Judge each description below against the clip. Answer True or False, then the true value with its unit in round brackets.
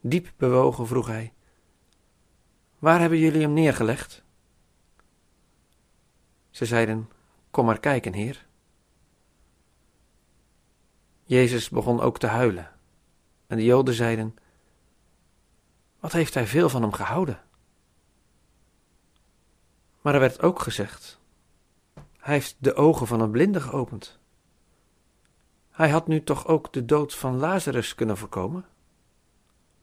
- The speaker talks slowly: True (110 wpm)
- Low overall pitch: True (115 Hz)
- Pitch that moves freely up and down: True (8.1 semitones)